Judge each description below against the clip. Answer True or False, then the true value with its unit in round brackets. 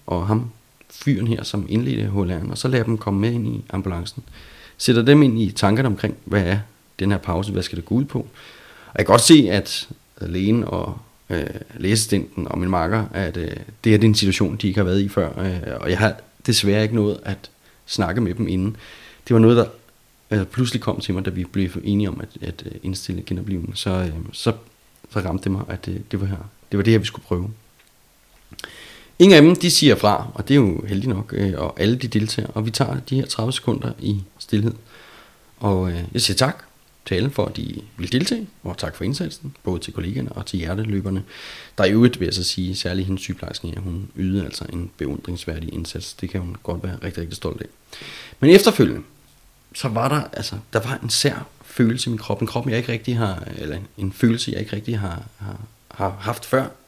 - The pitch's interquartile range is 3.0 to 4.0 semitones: True (3.7 semitones)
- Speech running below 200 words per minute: False (220 wpm)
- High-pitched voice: False (105 Hz)